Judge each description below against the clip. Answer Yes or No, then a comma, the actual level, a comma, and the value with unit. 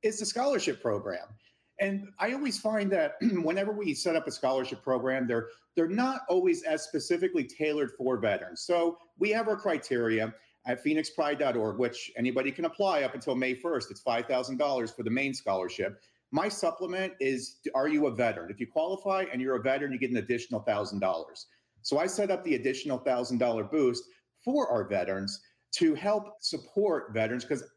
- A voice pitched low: No, medium, 155 Hz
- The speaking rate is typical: Yes, average, 175 wpm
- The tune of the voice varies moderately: No, wide, 8.8 semitones